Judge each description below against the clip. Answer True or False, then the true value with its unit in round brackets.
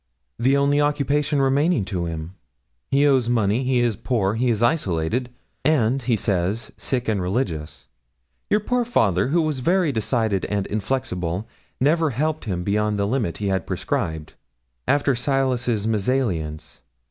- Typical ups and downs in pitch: False (5.7 semitones)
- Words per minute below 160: True (145 wpm)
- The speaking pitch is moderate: False (120 Hz)